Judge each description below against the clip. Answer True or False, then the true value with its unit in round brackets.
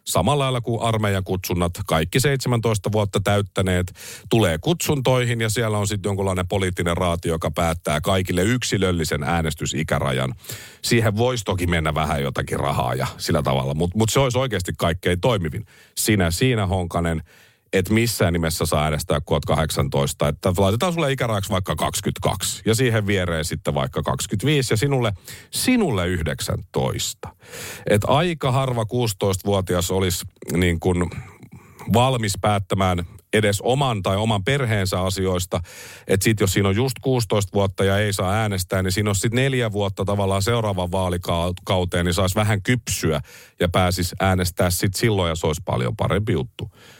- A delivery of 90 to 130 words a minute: False (150 wpm)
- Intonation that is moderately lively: True (4.3 semitones)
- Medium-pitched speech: False (100 Hz)